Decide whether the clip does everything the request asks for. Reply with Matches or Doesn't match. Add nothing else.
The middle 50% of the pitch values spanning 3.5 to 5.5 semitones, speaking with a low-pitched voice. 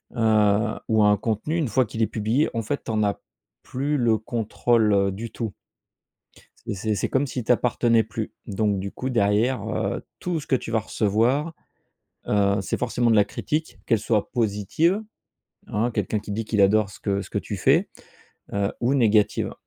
Doesn't match